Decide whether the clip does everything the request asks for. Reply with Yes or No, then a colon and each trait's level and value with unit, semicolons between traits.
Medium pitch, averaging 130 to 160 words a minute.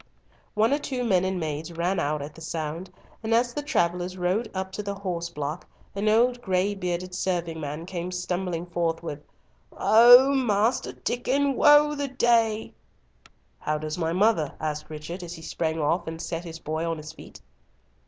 No: medium, 180 Hz; average, 185 wpm